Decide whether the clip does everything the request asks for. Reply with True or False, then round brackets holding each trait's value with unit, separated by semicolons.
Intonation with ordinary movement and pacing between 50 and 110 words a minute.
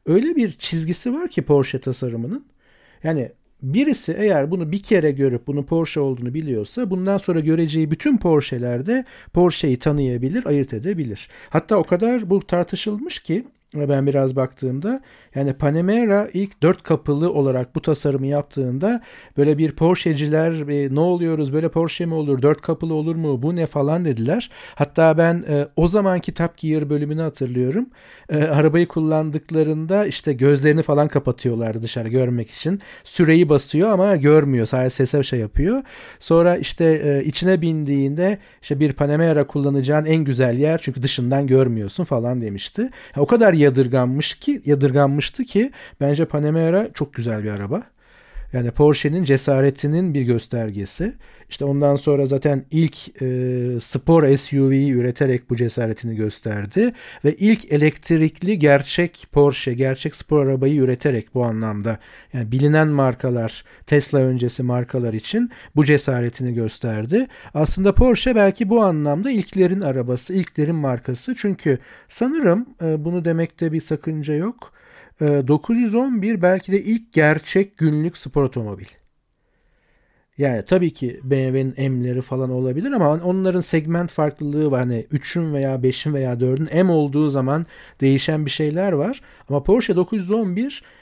False (4.9 semitones; 135 wpm)